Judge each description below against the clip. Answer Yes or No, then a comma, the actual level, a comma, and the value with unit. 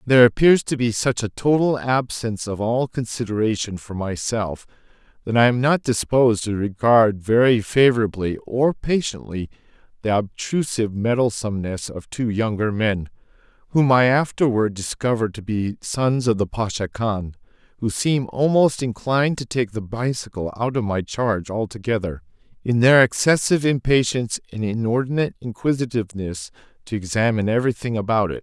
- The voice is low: Yes, low, 115 Hz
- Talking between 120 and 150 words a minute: Yes, average, 140 wpm